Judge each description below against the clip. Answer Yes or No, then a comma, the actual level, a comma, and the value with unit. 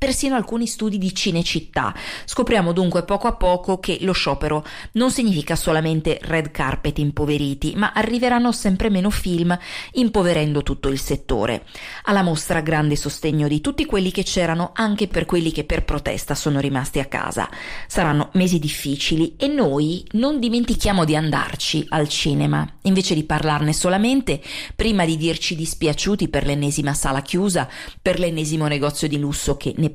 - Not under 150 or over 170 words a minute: Yes, average, 155 wpm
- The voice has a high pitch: No, medium, 165 Hz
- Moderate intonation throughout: Yes, average, 4.9 semitones